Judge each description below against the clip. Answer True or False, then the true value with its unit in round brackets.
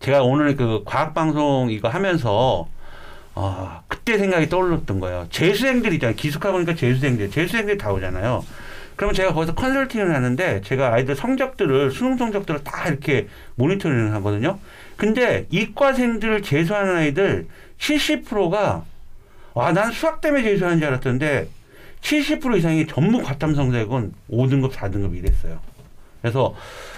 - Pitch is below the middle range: False (150 Hz)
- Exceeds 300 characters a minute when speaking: True (330 characters per minute)